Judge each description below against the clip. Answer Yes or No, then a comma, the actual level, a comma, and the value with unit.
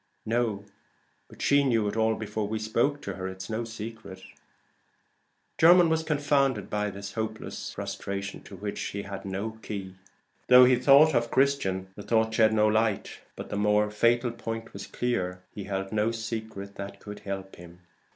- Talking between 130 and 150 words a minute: No, average, 170 wpm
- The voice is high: No, low, 110 Hz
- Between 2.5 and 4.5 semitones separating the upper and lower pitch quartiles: Yes, average, 2.9 semitones